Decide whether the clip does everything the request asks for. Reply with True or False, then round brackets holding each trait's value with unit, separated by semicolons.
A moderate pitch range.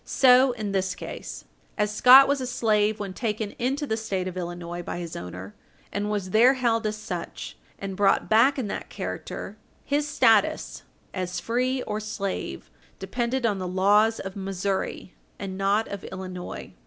True (3.9 semitones)